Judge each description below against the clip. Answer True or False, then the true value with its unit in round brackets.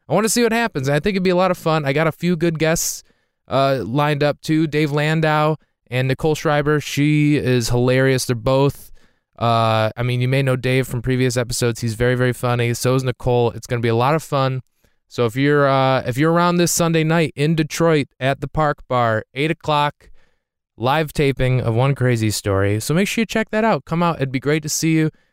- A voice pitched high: False (140 Hz)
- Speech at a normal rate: False (230 wpm)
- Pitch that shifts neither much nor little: True (4.1 semitones)